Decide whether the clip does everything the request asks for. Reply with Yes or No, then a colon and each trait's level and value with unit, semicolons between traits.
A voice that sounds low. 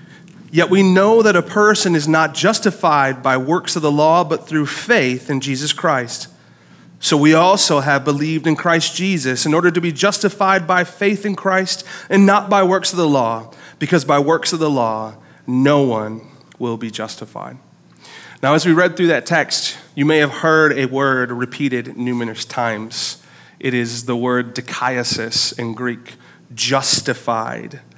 No: medium, 150 Hz